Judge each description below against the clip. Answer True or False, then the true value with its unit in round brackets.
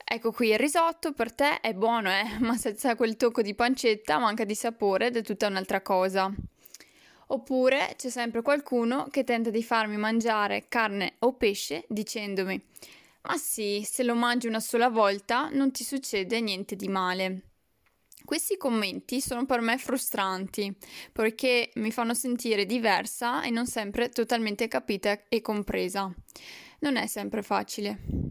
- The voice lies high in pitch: True (230 Hz)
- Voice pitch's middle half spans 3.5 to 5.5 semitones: False (3.0 semitones)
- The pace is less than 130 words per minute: False (155 wpm)